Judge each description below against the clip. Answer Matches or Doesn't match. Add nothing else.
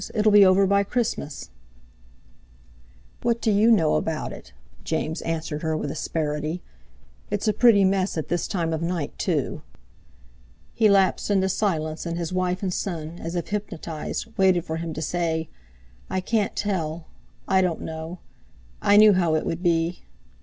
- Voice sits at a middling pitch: Matches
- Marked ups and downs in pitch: Doesn't match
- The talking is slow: Doesn't match